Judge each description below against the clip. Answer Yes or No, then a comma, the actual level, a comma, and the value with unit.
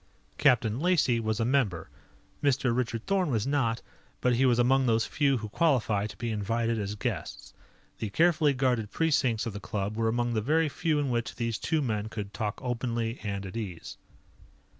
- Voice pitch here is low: Yes, low, 115 Hz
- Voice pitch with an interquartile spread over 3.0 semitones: Yes, average, 3.7 semitones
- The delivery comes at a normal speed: Yes, average, 185 wpm